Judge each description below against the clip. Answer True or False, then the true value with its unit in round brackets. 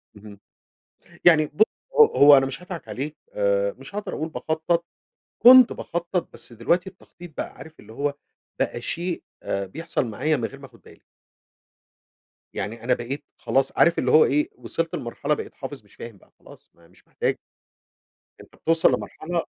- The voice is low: False (155 Hz)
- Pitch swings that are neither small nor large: False (5.7 semitones)